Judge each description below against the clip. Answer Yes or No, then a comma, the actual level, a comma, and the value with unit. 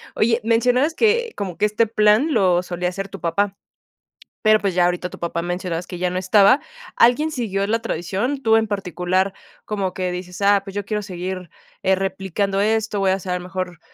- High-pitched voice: Yes, high, 195 Hz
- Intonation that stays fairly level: No, average, 3.2 semitones